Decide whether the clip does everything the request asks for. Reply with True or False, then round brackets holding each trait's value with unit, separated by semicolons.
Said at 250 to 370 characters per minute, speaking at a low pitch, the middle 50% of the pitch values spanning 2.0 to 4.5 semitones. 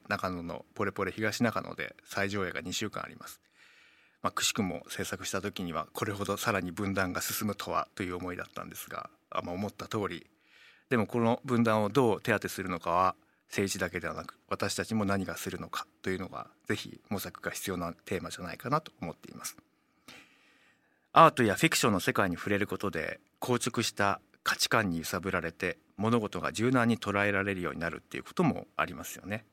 False (400 characters per minute; 100 Hz; 2.7 semitones)